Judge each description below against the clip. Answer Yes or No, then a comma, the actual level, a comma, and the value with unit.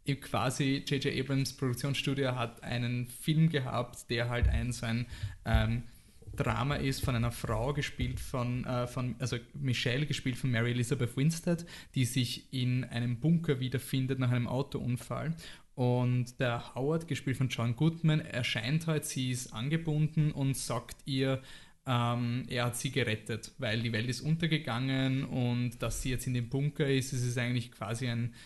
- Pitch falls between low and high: No, low, 125 Hz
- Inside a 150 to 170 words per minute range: Yes, average, 160 wpm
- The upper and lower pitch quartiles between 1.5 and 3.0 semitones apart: Yes, narrow, 2.6 semitones